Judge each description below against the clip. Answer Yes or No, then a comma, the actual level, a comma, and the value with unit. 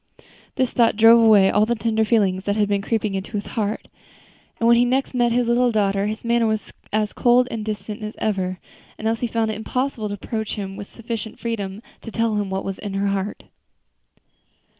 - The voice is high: Yes, high, 220 Hz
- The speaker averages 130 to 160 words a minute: No, fast, 205 wpm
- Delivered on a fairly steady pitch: Yes, narrow, 2.3 semitones